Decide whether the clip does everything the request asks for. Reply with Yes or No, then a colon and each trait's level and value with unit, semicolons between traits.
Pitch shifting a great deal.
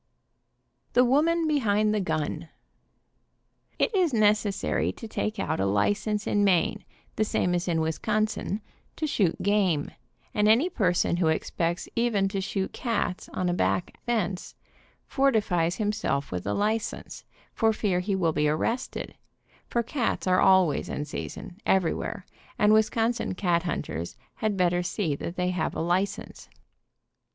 No: average, 3.9 semitones